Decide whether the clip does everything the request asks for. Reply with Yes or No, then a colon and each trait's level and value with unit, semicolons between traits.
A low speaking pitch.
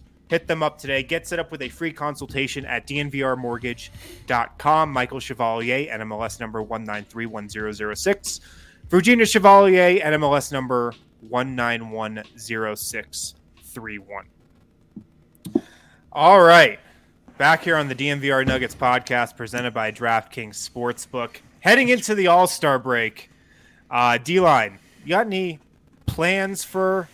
Yes: low, 125 Hz